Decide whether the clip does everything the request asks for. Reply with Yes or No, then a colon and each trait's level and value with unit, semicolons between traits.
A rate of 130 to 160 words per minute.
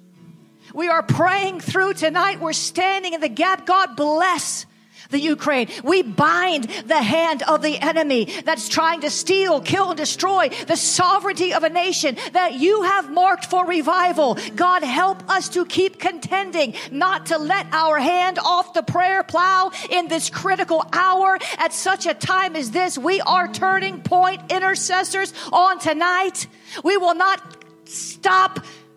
Yes: average, 155 wpm